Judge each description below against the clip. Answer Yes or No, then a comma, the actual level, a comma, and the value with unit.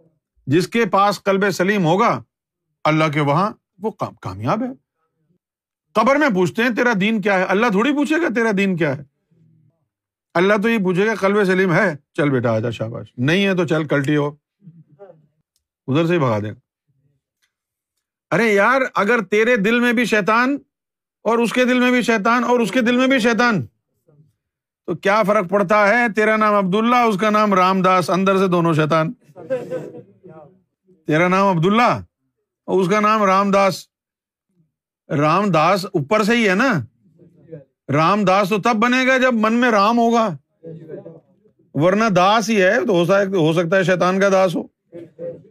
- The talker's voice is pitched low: No, high, 190 Hz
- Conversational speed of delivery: Yes, average, 170 wpm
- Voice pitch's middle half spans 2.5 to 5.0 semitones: No, wide, 5.5 semitones